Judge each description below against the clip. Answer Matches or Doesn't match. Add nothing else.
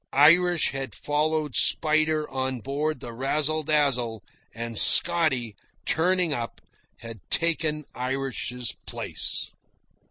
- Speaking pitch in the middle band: Matches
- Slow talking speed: Matches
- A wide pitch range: Doesn't match